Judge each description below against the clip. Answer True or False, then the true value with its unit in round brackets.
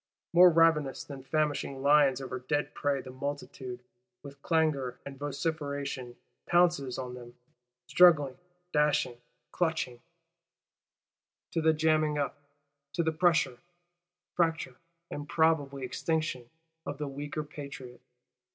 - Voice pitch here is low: False (145 Hz)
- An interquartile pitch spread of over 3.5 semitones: False (3.2 semitones)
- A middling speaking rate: False (110 wpm)